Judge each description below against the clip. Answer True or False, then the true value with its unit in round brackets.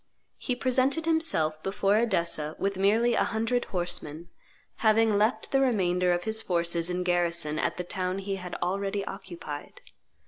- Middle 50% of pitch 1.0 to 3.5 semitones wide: False (4.1 semitones)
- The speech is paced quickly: False (150 wpm)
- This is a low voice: False (195 Hz)